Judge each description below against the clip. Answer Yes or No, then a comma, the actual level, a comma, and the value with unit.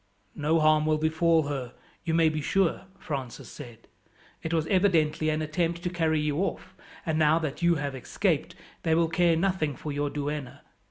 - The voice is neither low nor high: Yes, medium, 155 Hz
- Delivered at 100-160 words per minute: No, average, 180 wpm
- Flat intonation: Yes, narrow, 2.1 semitones